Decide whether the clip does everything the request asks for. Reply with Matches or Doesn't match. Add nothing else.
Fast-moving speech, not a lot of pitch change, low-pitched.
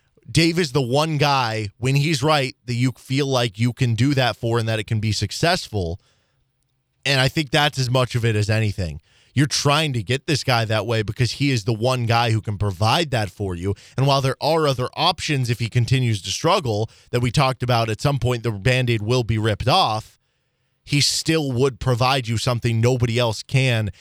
Doesn't match